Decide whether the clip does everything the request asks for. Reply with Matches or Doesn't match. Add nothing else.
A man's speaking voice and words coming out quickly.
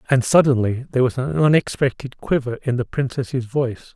Doesn't match